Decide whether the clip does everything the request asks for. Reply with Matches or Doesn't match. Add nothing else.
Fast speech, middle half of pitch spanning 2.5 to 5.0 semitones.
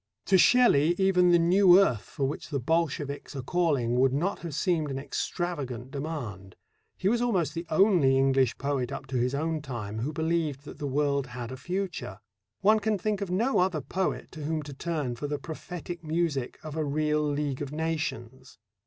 Doesn't match